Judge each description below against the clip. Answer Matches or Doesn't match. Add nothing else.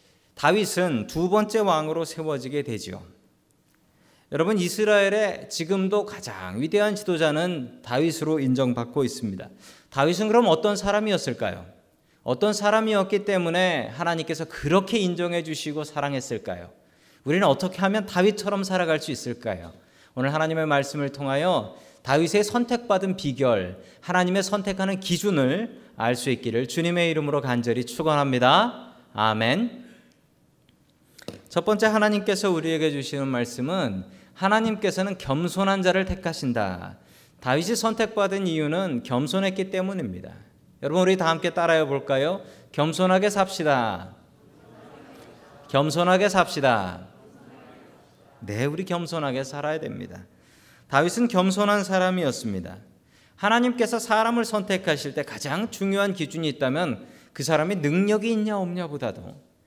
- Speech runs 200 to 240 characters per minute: Doesn't match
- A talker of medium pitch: Matches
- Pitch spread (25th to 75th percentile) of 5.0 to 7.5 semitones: Matches